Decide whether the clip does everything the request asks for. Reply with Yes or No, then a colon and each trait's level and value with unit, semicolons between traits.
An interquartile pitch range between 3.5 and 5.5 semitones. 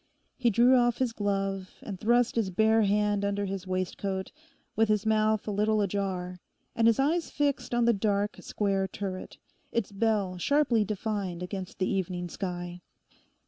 No: average, 2.9 semitones